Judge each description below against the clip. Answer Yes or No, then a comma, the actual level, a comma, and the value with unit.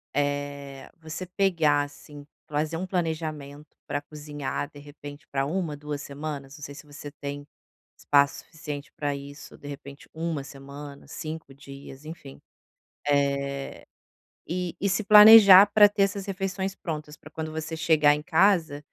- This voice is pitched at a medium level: Yes, medium, 150 Hz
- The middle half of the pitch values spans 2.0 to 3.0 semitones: Yes, narrow, 2.6 semitones